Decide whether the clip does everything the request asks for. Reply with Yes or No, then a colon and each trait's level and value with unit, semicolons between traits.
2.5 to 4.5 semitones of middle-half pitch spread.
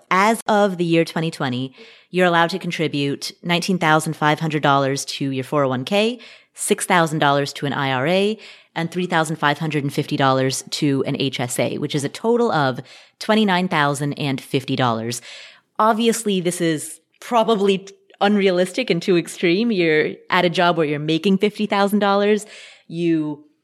No: wide, 5.6 semitones